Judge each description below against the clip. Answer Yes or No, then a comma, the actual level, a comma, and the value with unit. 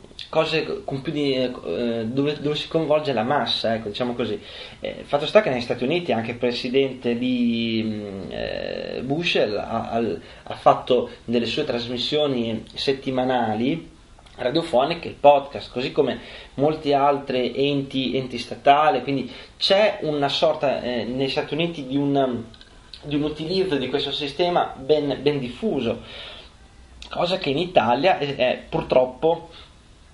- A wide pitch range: No, average, 3.3 semitones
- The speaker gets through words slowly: No, average, 145 wpm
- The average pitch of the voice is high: No, low, 135 Hz